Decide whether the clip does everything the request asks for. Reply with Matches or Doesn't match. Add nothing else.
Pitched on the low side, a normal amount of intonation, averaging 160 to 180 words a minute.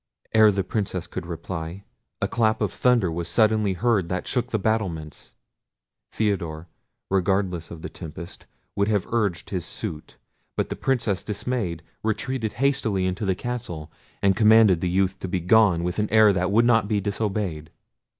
Matches